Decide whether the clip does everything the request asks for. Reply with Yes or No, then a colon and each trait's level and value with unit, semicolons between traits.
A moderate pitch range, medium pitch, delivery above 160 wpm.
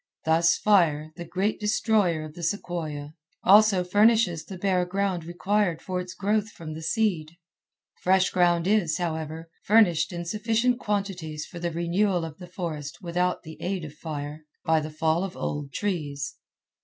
No: average, 3.8 semitones; medium, 175 Hz; average, 155 wpm